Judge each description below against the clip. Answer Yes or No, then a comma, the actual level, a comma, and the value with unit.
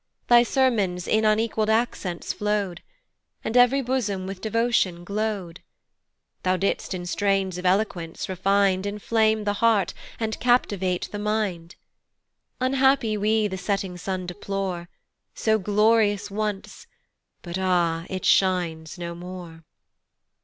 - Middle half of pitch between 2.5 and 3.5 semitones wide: Yes, average, 3.1 semitones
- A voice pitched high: Yes, high, 200 Hz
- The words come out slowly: Yes, slow, 120 wpm